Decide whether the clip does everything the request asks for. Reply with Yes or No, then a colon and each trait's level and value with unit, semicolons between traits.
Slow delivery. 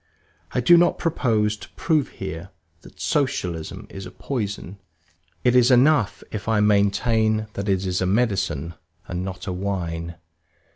No: average, 150 wpm